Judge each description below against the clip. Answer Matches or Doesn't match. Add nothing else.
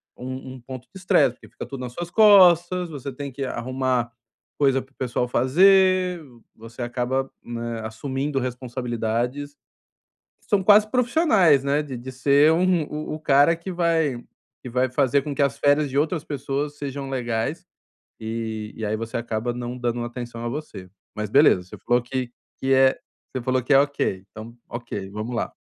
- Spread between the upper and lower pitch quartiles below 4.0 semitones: Matches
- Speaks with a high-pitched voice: Doesn't match